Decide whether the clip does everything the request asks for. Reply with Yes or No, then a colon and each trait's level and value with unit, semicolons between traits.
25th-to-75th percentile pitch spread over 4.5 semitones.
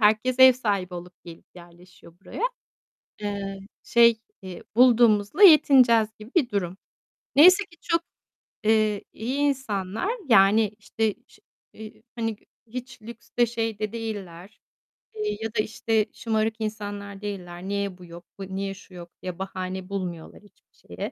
No: average, 3.3 semitones